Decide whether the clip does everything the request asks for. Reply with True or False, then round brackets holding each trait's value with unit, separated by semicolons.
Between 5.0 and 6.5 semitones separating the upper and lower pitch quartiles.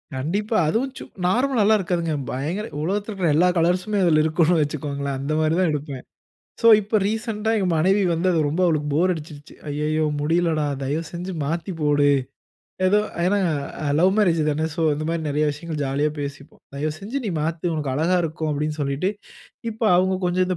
False (3.8 semitones)